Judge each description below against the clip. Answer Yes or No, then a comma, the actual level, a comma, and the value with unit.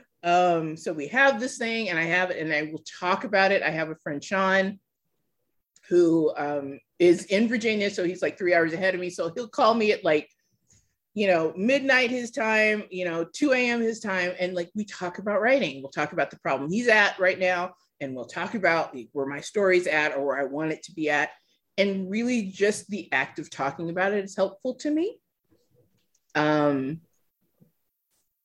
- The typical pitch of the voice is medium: Yes, medium, 180 Hz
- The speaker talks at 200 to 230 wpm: Yes, fast, 205 wpm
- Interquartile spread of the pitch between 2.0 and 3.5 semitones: No, average, 5.0 semitones